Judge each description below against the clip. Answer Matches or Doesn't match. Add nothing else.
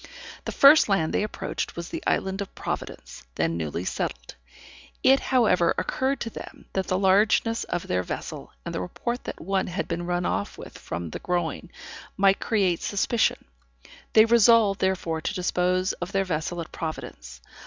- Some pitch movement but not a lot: Matches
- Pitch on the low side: Doesn't match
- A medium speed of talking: Matches